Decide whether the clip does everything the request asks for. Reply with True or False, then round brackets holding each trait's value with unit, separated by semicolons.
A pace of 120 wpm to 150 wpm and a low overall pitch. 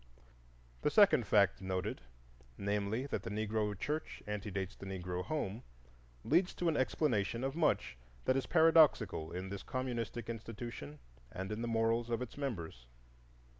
True (145 wpm; 115 Hz)